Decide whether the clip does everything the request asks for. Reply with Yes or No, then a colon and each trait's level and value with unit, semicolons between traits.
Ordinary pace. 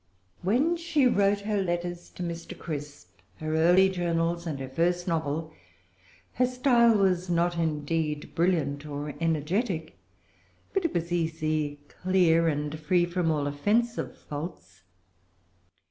No: slow, 130 wpm